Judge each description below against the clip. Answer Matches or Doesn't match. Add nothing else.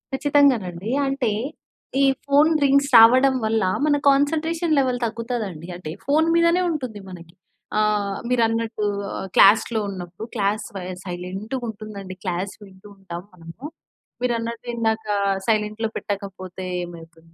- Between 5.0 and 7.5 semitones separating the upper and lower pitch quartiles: Matches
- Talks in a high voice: Matches